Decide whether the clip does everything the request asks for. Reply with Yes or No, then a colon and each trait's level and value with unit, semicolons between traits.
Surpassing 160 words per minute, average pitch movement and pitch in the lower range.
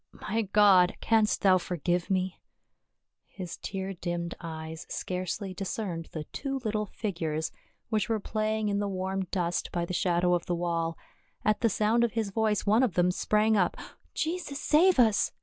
No: average, 175 wpm; average, 3.6 semitones; high, 195 Hz